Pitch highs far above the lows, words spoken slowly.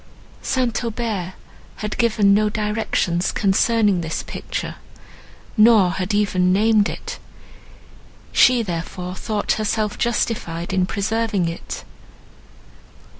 No: average, 3.4 semitones; slow, 100 wpm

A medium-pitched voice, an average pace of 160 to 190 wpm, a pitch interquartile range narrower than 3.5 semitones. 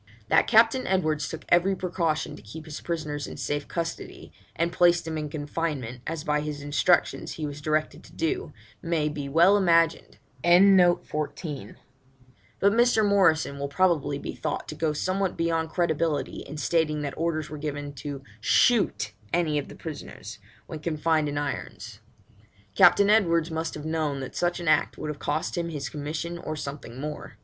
Yes: medium, 155 Hz; average, 170 wpm; average, 2.8 semitones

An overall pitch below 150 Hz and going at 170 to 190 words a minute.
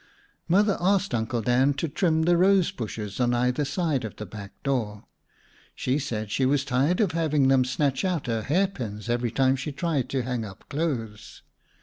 Yes: low, 135 Hz; average, 185 wpm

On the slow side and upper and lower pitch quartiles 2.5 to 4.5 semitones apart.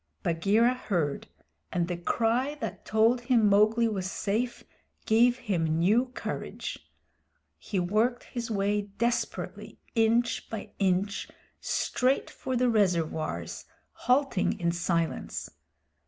No: slow, 110 wpm; average, 4.9 semitones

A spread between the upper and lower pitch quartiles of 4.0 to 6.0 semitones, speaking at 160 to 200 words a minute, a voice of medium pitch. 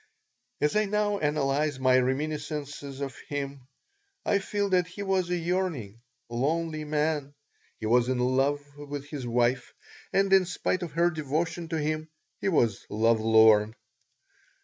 No: average, 4.7 semitones; average, 150 wpm; medium, 145 Hz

